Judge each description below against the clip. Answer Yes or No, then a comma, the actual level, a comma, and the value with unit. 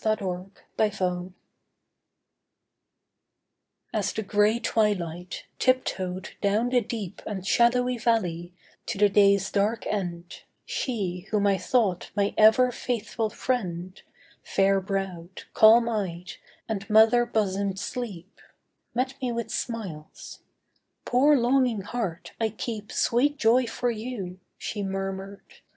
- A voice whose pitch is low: No, high, 210 Hz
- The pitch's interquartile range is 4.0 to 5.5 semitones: No, average, 3.6 semitones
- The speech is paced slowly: Yes, slow, 115 wpm